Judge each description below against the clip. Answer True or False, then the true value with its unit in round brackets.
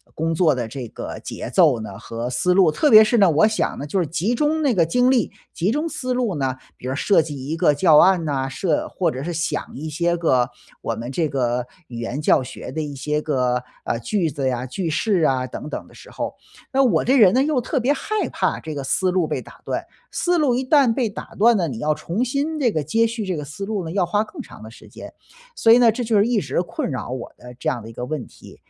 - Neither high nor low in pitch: True (165 Hz)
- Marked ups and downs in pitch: True (8.9 semitones)